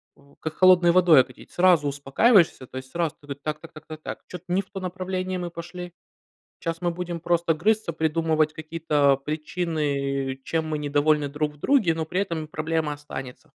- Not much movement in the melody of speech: No, average, 3.1 semitones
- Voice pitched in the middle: Yes, medium, 160 Hz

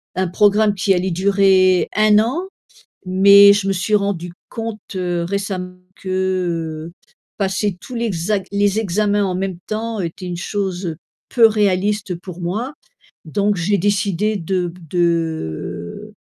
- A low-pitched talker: No, high, 190 Hz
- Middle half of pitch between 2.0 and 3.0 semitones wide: Yes, narrow, 2.5 semitones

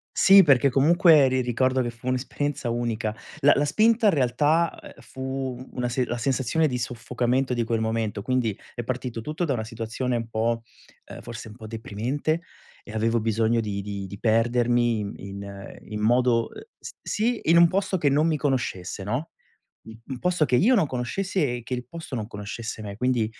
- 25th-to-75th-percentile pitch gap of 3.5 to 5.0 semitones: Yes, average, 4.1 semitones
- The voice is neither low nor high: No, low, 125 Hz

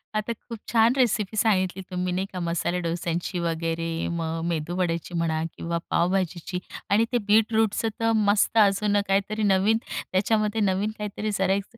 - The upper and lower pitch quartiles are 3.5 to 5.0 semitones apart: Yes, average, 3.8 semitones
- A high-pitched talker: Yes, high, 195 Hz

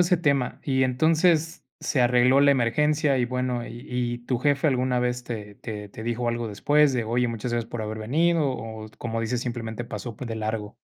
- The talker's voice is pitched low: Yes, low, 125 Hz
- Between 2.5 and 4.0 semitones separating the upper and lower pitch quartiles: Yes, average, 3.2 semitones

